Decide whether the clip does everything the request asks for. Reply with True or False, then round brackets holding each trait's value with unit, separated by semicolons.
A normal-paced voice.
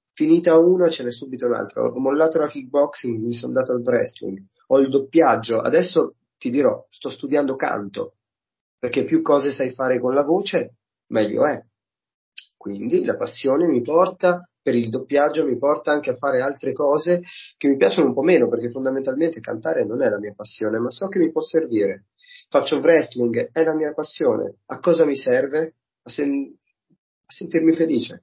False (180 wpm)